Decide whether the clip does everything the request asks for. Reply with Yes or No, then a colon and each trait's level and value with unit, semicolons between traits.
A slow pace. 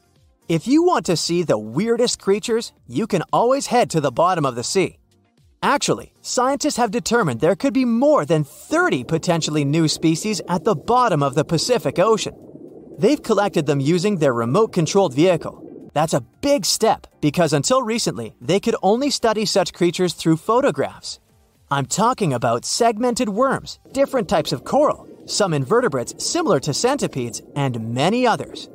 No: average, 165 wpm